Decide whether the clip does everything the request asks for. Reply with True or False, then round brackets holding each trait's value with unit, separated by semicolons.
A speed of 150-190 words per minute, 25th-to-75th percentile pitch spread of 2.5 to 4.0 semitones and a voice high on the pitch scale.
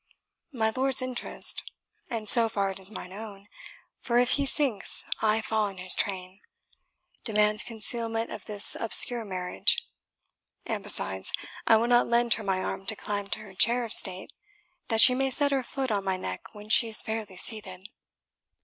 True (175 wpm; 3.3 semitones; 220 Hz)